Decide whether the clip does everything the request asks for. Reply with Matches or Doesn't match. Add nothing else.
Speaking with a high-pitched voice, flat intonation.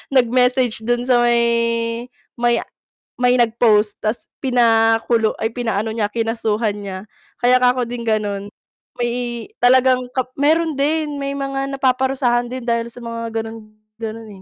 Matches